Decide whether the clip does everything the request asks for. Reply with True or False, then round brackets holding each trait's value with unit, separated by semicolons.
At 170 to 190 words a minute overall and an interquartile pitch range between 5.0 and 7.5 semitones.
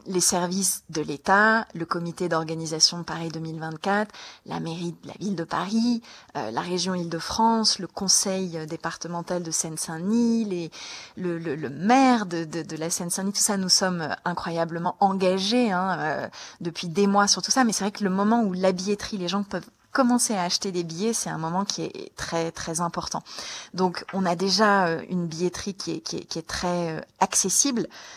False (185 wpm; 3.1 semitones)